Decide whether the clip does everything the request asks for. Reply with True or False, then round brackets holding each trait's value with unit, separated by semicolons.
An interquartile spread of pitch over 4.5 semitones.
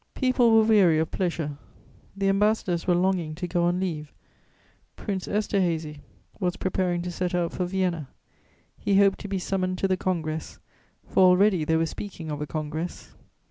False (3.0 semitones)